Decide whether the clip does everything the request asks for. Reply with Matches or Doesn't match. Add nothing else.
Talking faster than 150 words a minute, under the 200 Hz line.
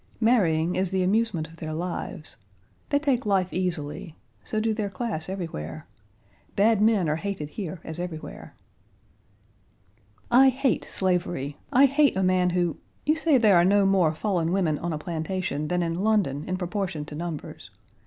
Matches